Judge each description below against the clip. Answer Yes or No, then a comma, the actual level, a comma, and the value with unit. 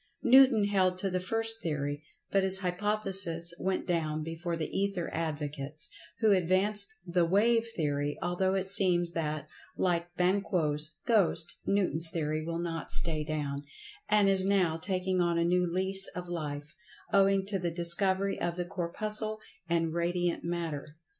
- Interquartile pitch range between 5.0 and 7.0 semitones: No, average, 2.9 semitones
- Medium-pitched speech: Yes, medium, 175 Hz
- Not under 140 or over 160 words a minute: Yes, average, 150 wpm